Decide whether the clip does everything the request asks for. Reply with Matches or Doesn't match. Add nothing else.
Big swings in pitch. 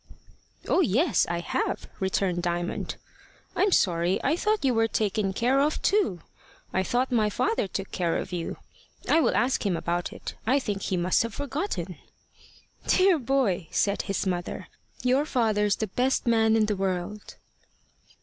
Matches